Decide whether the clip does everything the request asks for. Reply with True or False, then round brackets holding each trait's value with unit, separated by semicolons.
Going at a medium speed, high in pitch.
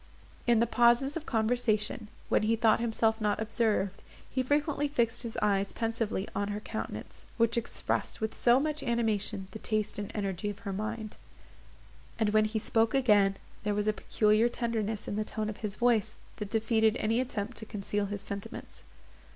True (175 wpm; 220 Hz)